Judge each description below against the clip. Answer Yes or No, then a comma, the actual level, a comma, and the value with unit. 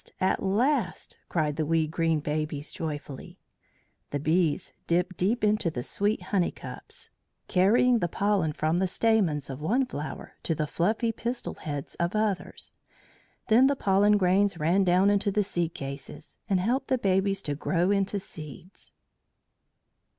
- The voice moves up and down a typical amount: Yes, average, 4.7 semitones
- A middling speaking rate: Yes, average, 150 wpm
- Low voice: No, medium, 185 Hz